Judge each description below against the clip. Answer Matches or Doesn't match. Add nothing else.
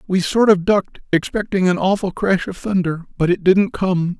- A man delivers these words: Matches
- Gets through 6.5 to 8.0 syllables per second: Doesn't match